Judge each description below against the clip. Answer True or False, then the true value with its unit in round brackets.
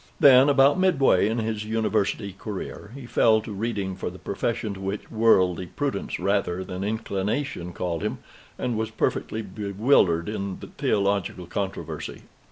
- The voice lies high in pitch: False (105 Hz)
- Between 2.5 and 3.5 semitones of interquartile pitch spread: True (2.9 semitones)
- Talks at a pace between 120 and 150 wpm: True (145 wpm)